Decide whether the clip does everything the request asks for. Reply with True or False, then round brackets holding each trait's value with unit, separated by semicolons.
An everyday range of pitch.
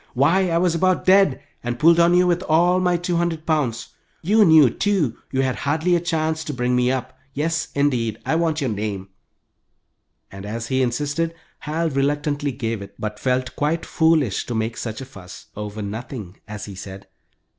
False (6.1 semitones)